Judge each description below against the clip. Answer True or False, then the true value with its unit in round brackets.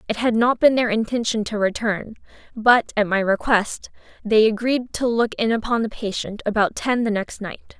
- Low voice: False (220 Hz)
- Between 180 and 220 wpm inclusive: True (190 wpm)